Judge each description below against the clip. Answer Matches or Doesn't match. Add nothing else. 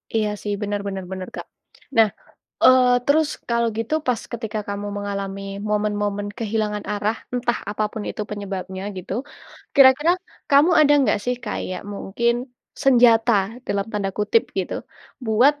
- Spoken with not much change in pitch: Doesn't match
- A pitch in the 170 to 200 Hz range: Doesn't match